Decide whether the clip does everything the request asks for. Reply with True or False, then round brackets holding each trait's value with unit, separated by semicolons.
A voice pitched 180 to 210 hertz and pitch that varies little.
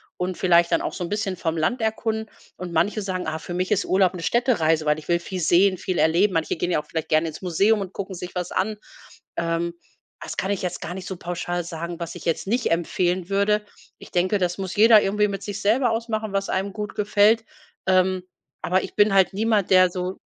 False (185 Hz; 3.1 semitones)